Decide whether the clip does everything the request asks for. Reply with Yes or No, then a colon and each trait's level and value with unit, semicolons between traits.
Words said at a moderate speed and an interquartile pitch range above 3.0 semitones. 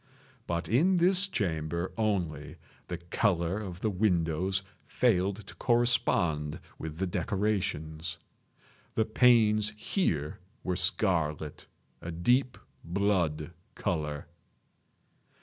No: slow, 95 wpm; average, 4.8 semitones